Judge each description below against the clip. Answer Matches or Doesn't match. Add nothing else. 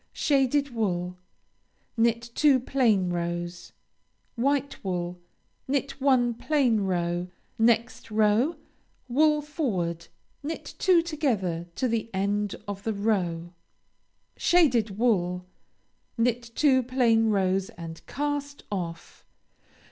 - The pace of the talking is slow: Matches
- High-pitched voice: Matches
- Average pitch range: Doesn't match